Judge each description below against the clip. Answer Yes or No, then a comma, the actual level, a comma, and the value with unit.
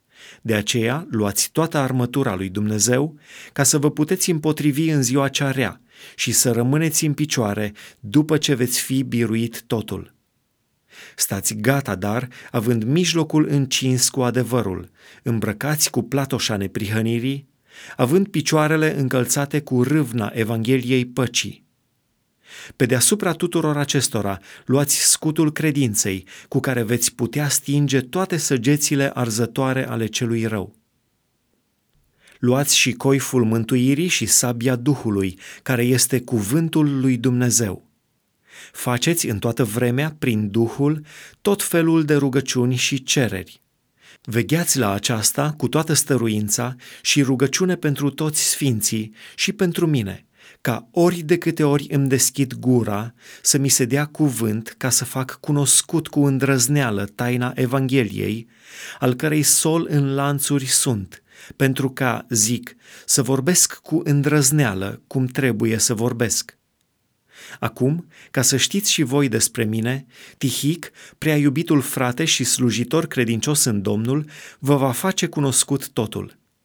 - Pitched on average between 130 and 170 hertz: Yes, low, 135 Hz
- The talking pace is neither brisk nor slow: Yes, average, 125 wpm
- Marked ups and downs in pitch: No, average, 3.8 semitones